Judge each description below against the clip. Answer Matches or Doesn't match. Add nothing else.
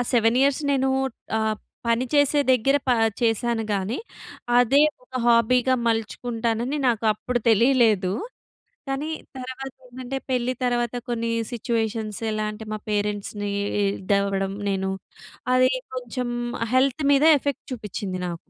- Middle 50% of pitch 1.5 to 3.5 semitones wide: Matches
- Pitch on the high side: Matches